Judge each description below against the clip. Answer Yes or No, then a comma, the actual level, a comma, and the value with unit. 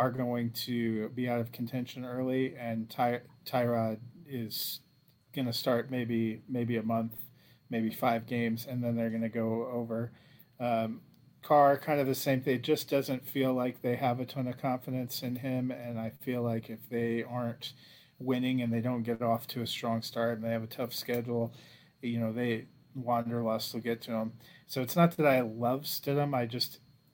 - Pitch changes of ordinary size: No, narrow, 2.1 semitones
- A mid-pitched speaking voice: No, low, 120 Hz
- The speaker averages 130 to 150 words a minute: No, average, 200 wpm